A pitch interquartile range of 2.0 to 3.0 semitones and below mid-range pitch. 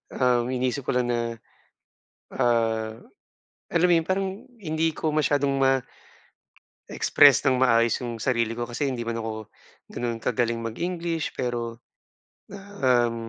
No: average, 3.7 semitones; low, 120 Hz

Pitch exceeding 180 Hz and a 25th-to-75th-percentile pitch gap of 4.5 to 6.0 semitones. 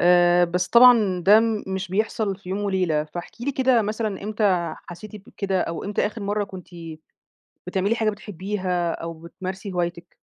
No: high, 190 Hz; average, 3.2 semitones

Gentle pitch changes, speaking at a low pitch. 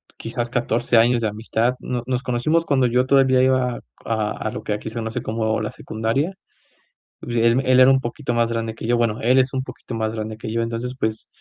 Yes: narrow, 2.3 semitones; low, 120 Hz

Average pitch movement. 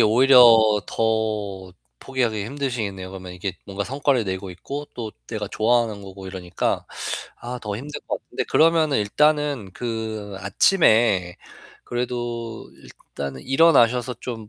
Yes: average, 4.2 semitones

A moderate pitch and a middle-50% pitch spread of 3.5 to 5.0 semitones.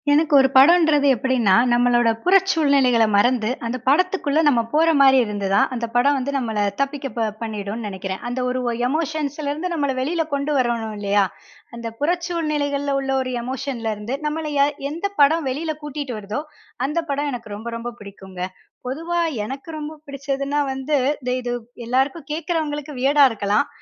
No: very high, 275 Hz; average, 4.1 semitones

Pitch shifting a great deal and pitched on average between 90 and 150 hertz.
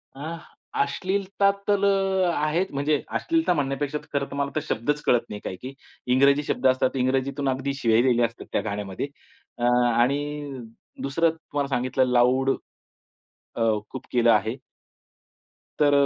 No: average, 2.9 semitones; medium, 140 Hz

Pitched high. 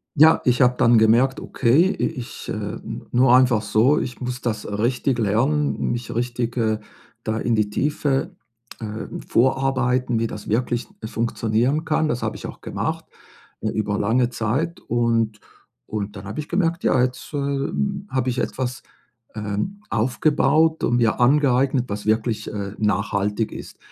No: low, 120 Hz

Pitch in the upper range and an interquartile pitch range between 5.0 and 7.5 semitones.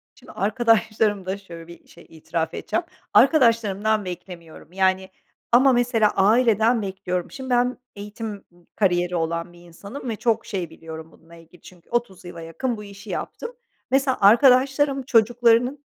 Yes: high, 205 Hz; wide, 5.4 semitones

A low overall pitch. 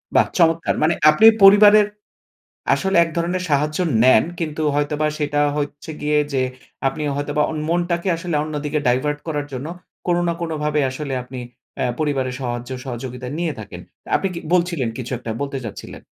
No: medium, 150 Hz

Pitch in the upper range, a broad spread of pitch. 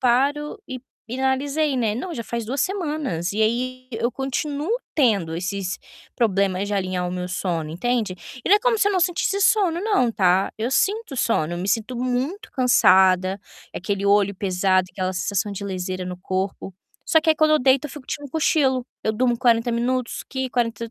Yes: high, 235 Hz; wide, 6.7 semitones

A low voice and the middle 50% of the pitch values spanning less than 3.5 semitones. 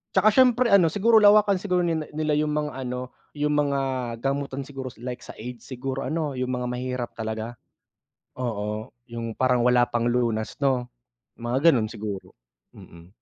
No: low, 130 Hz; average, 4.2 semitones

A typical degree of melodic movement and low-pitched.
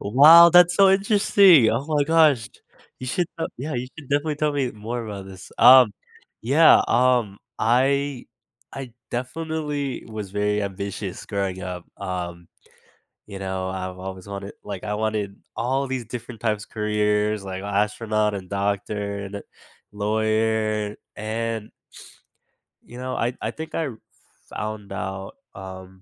Yes: average, 4.8 semitones; low, 110 Hz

